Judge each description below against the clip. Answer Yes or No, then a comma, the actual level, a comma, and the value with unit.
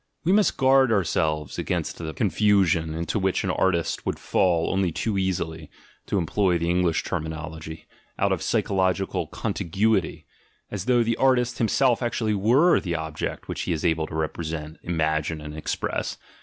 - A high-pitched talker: No, very low, 90 Hz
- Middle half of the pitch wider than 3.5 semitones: Yes, average, 5.0 semitones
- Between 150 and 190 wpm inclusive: Yes, average, 170 wpm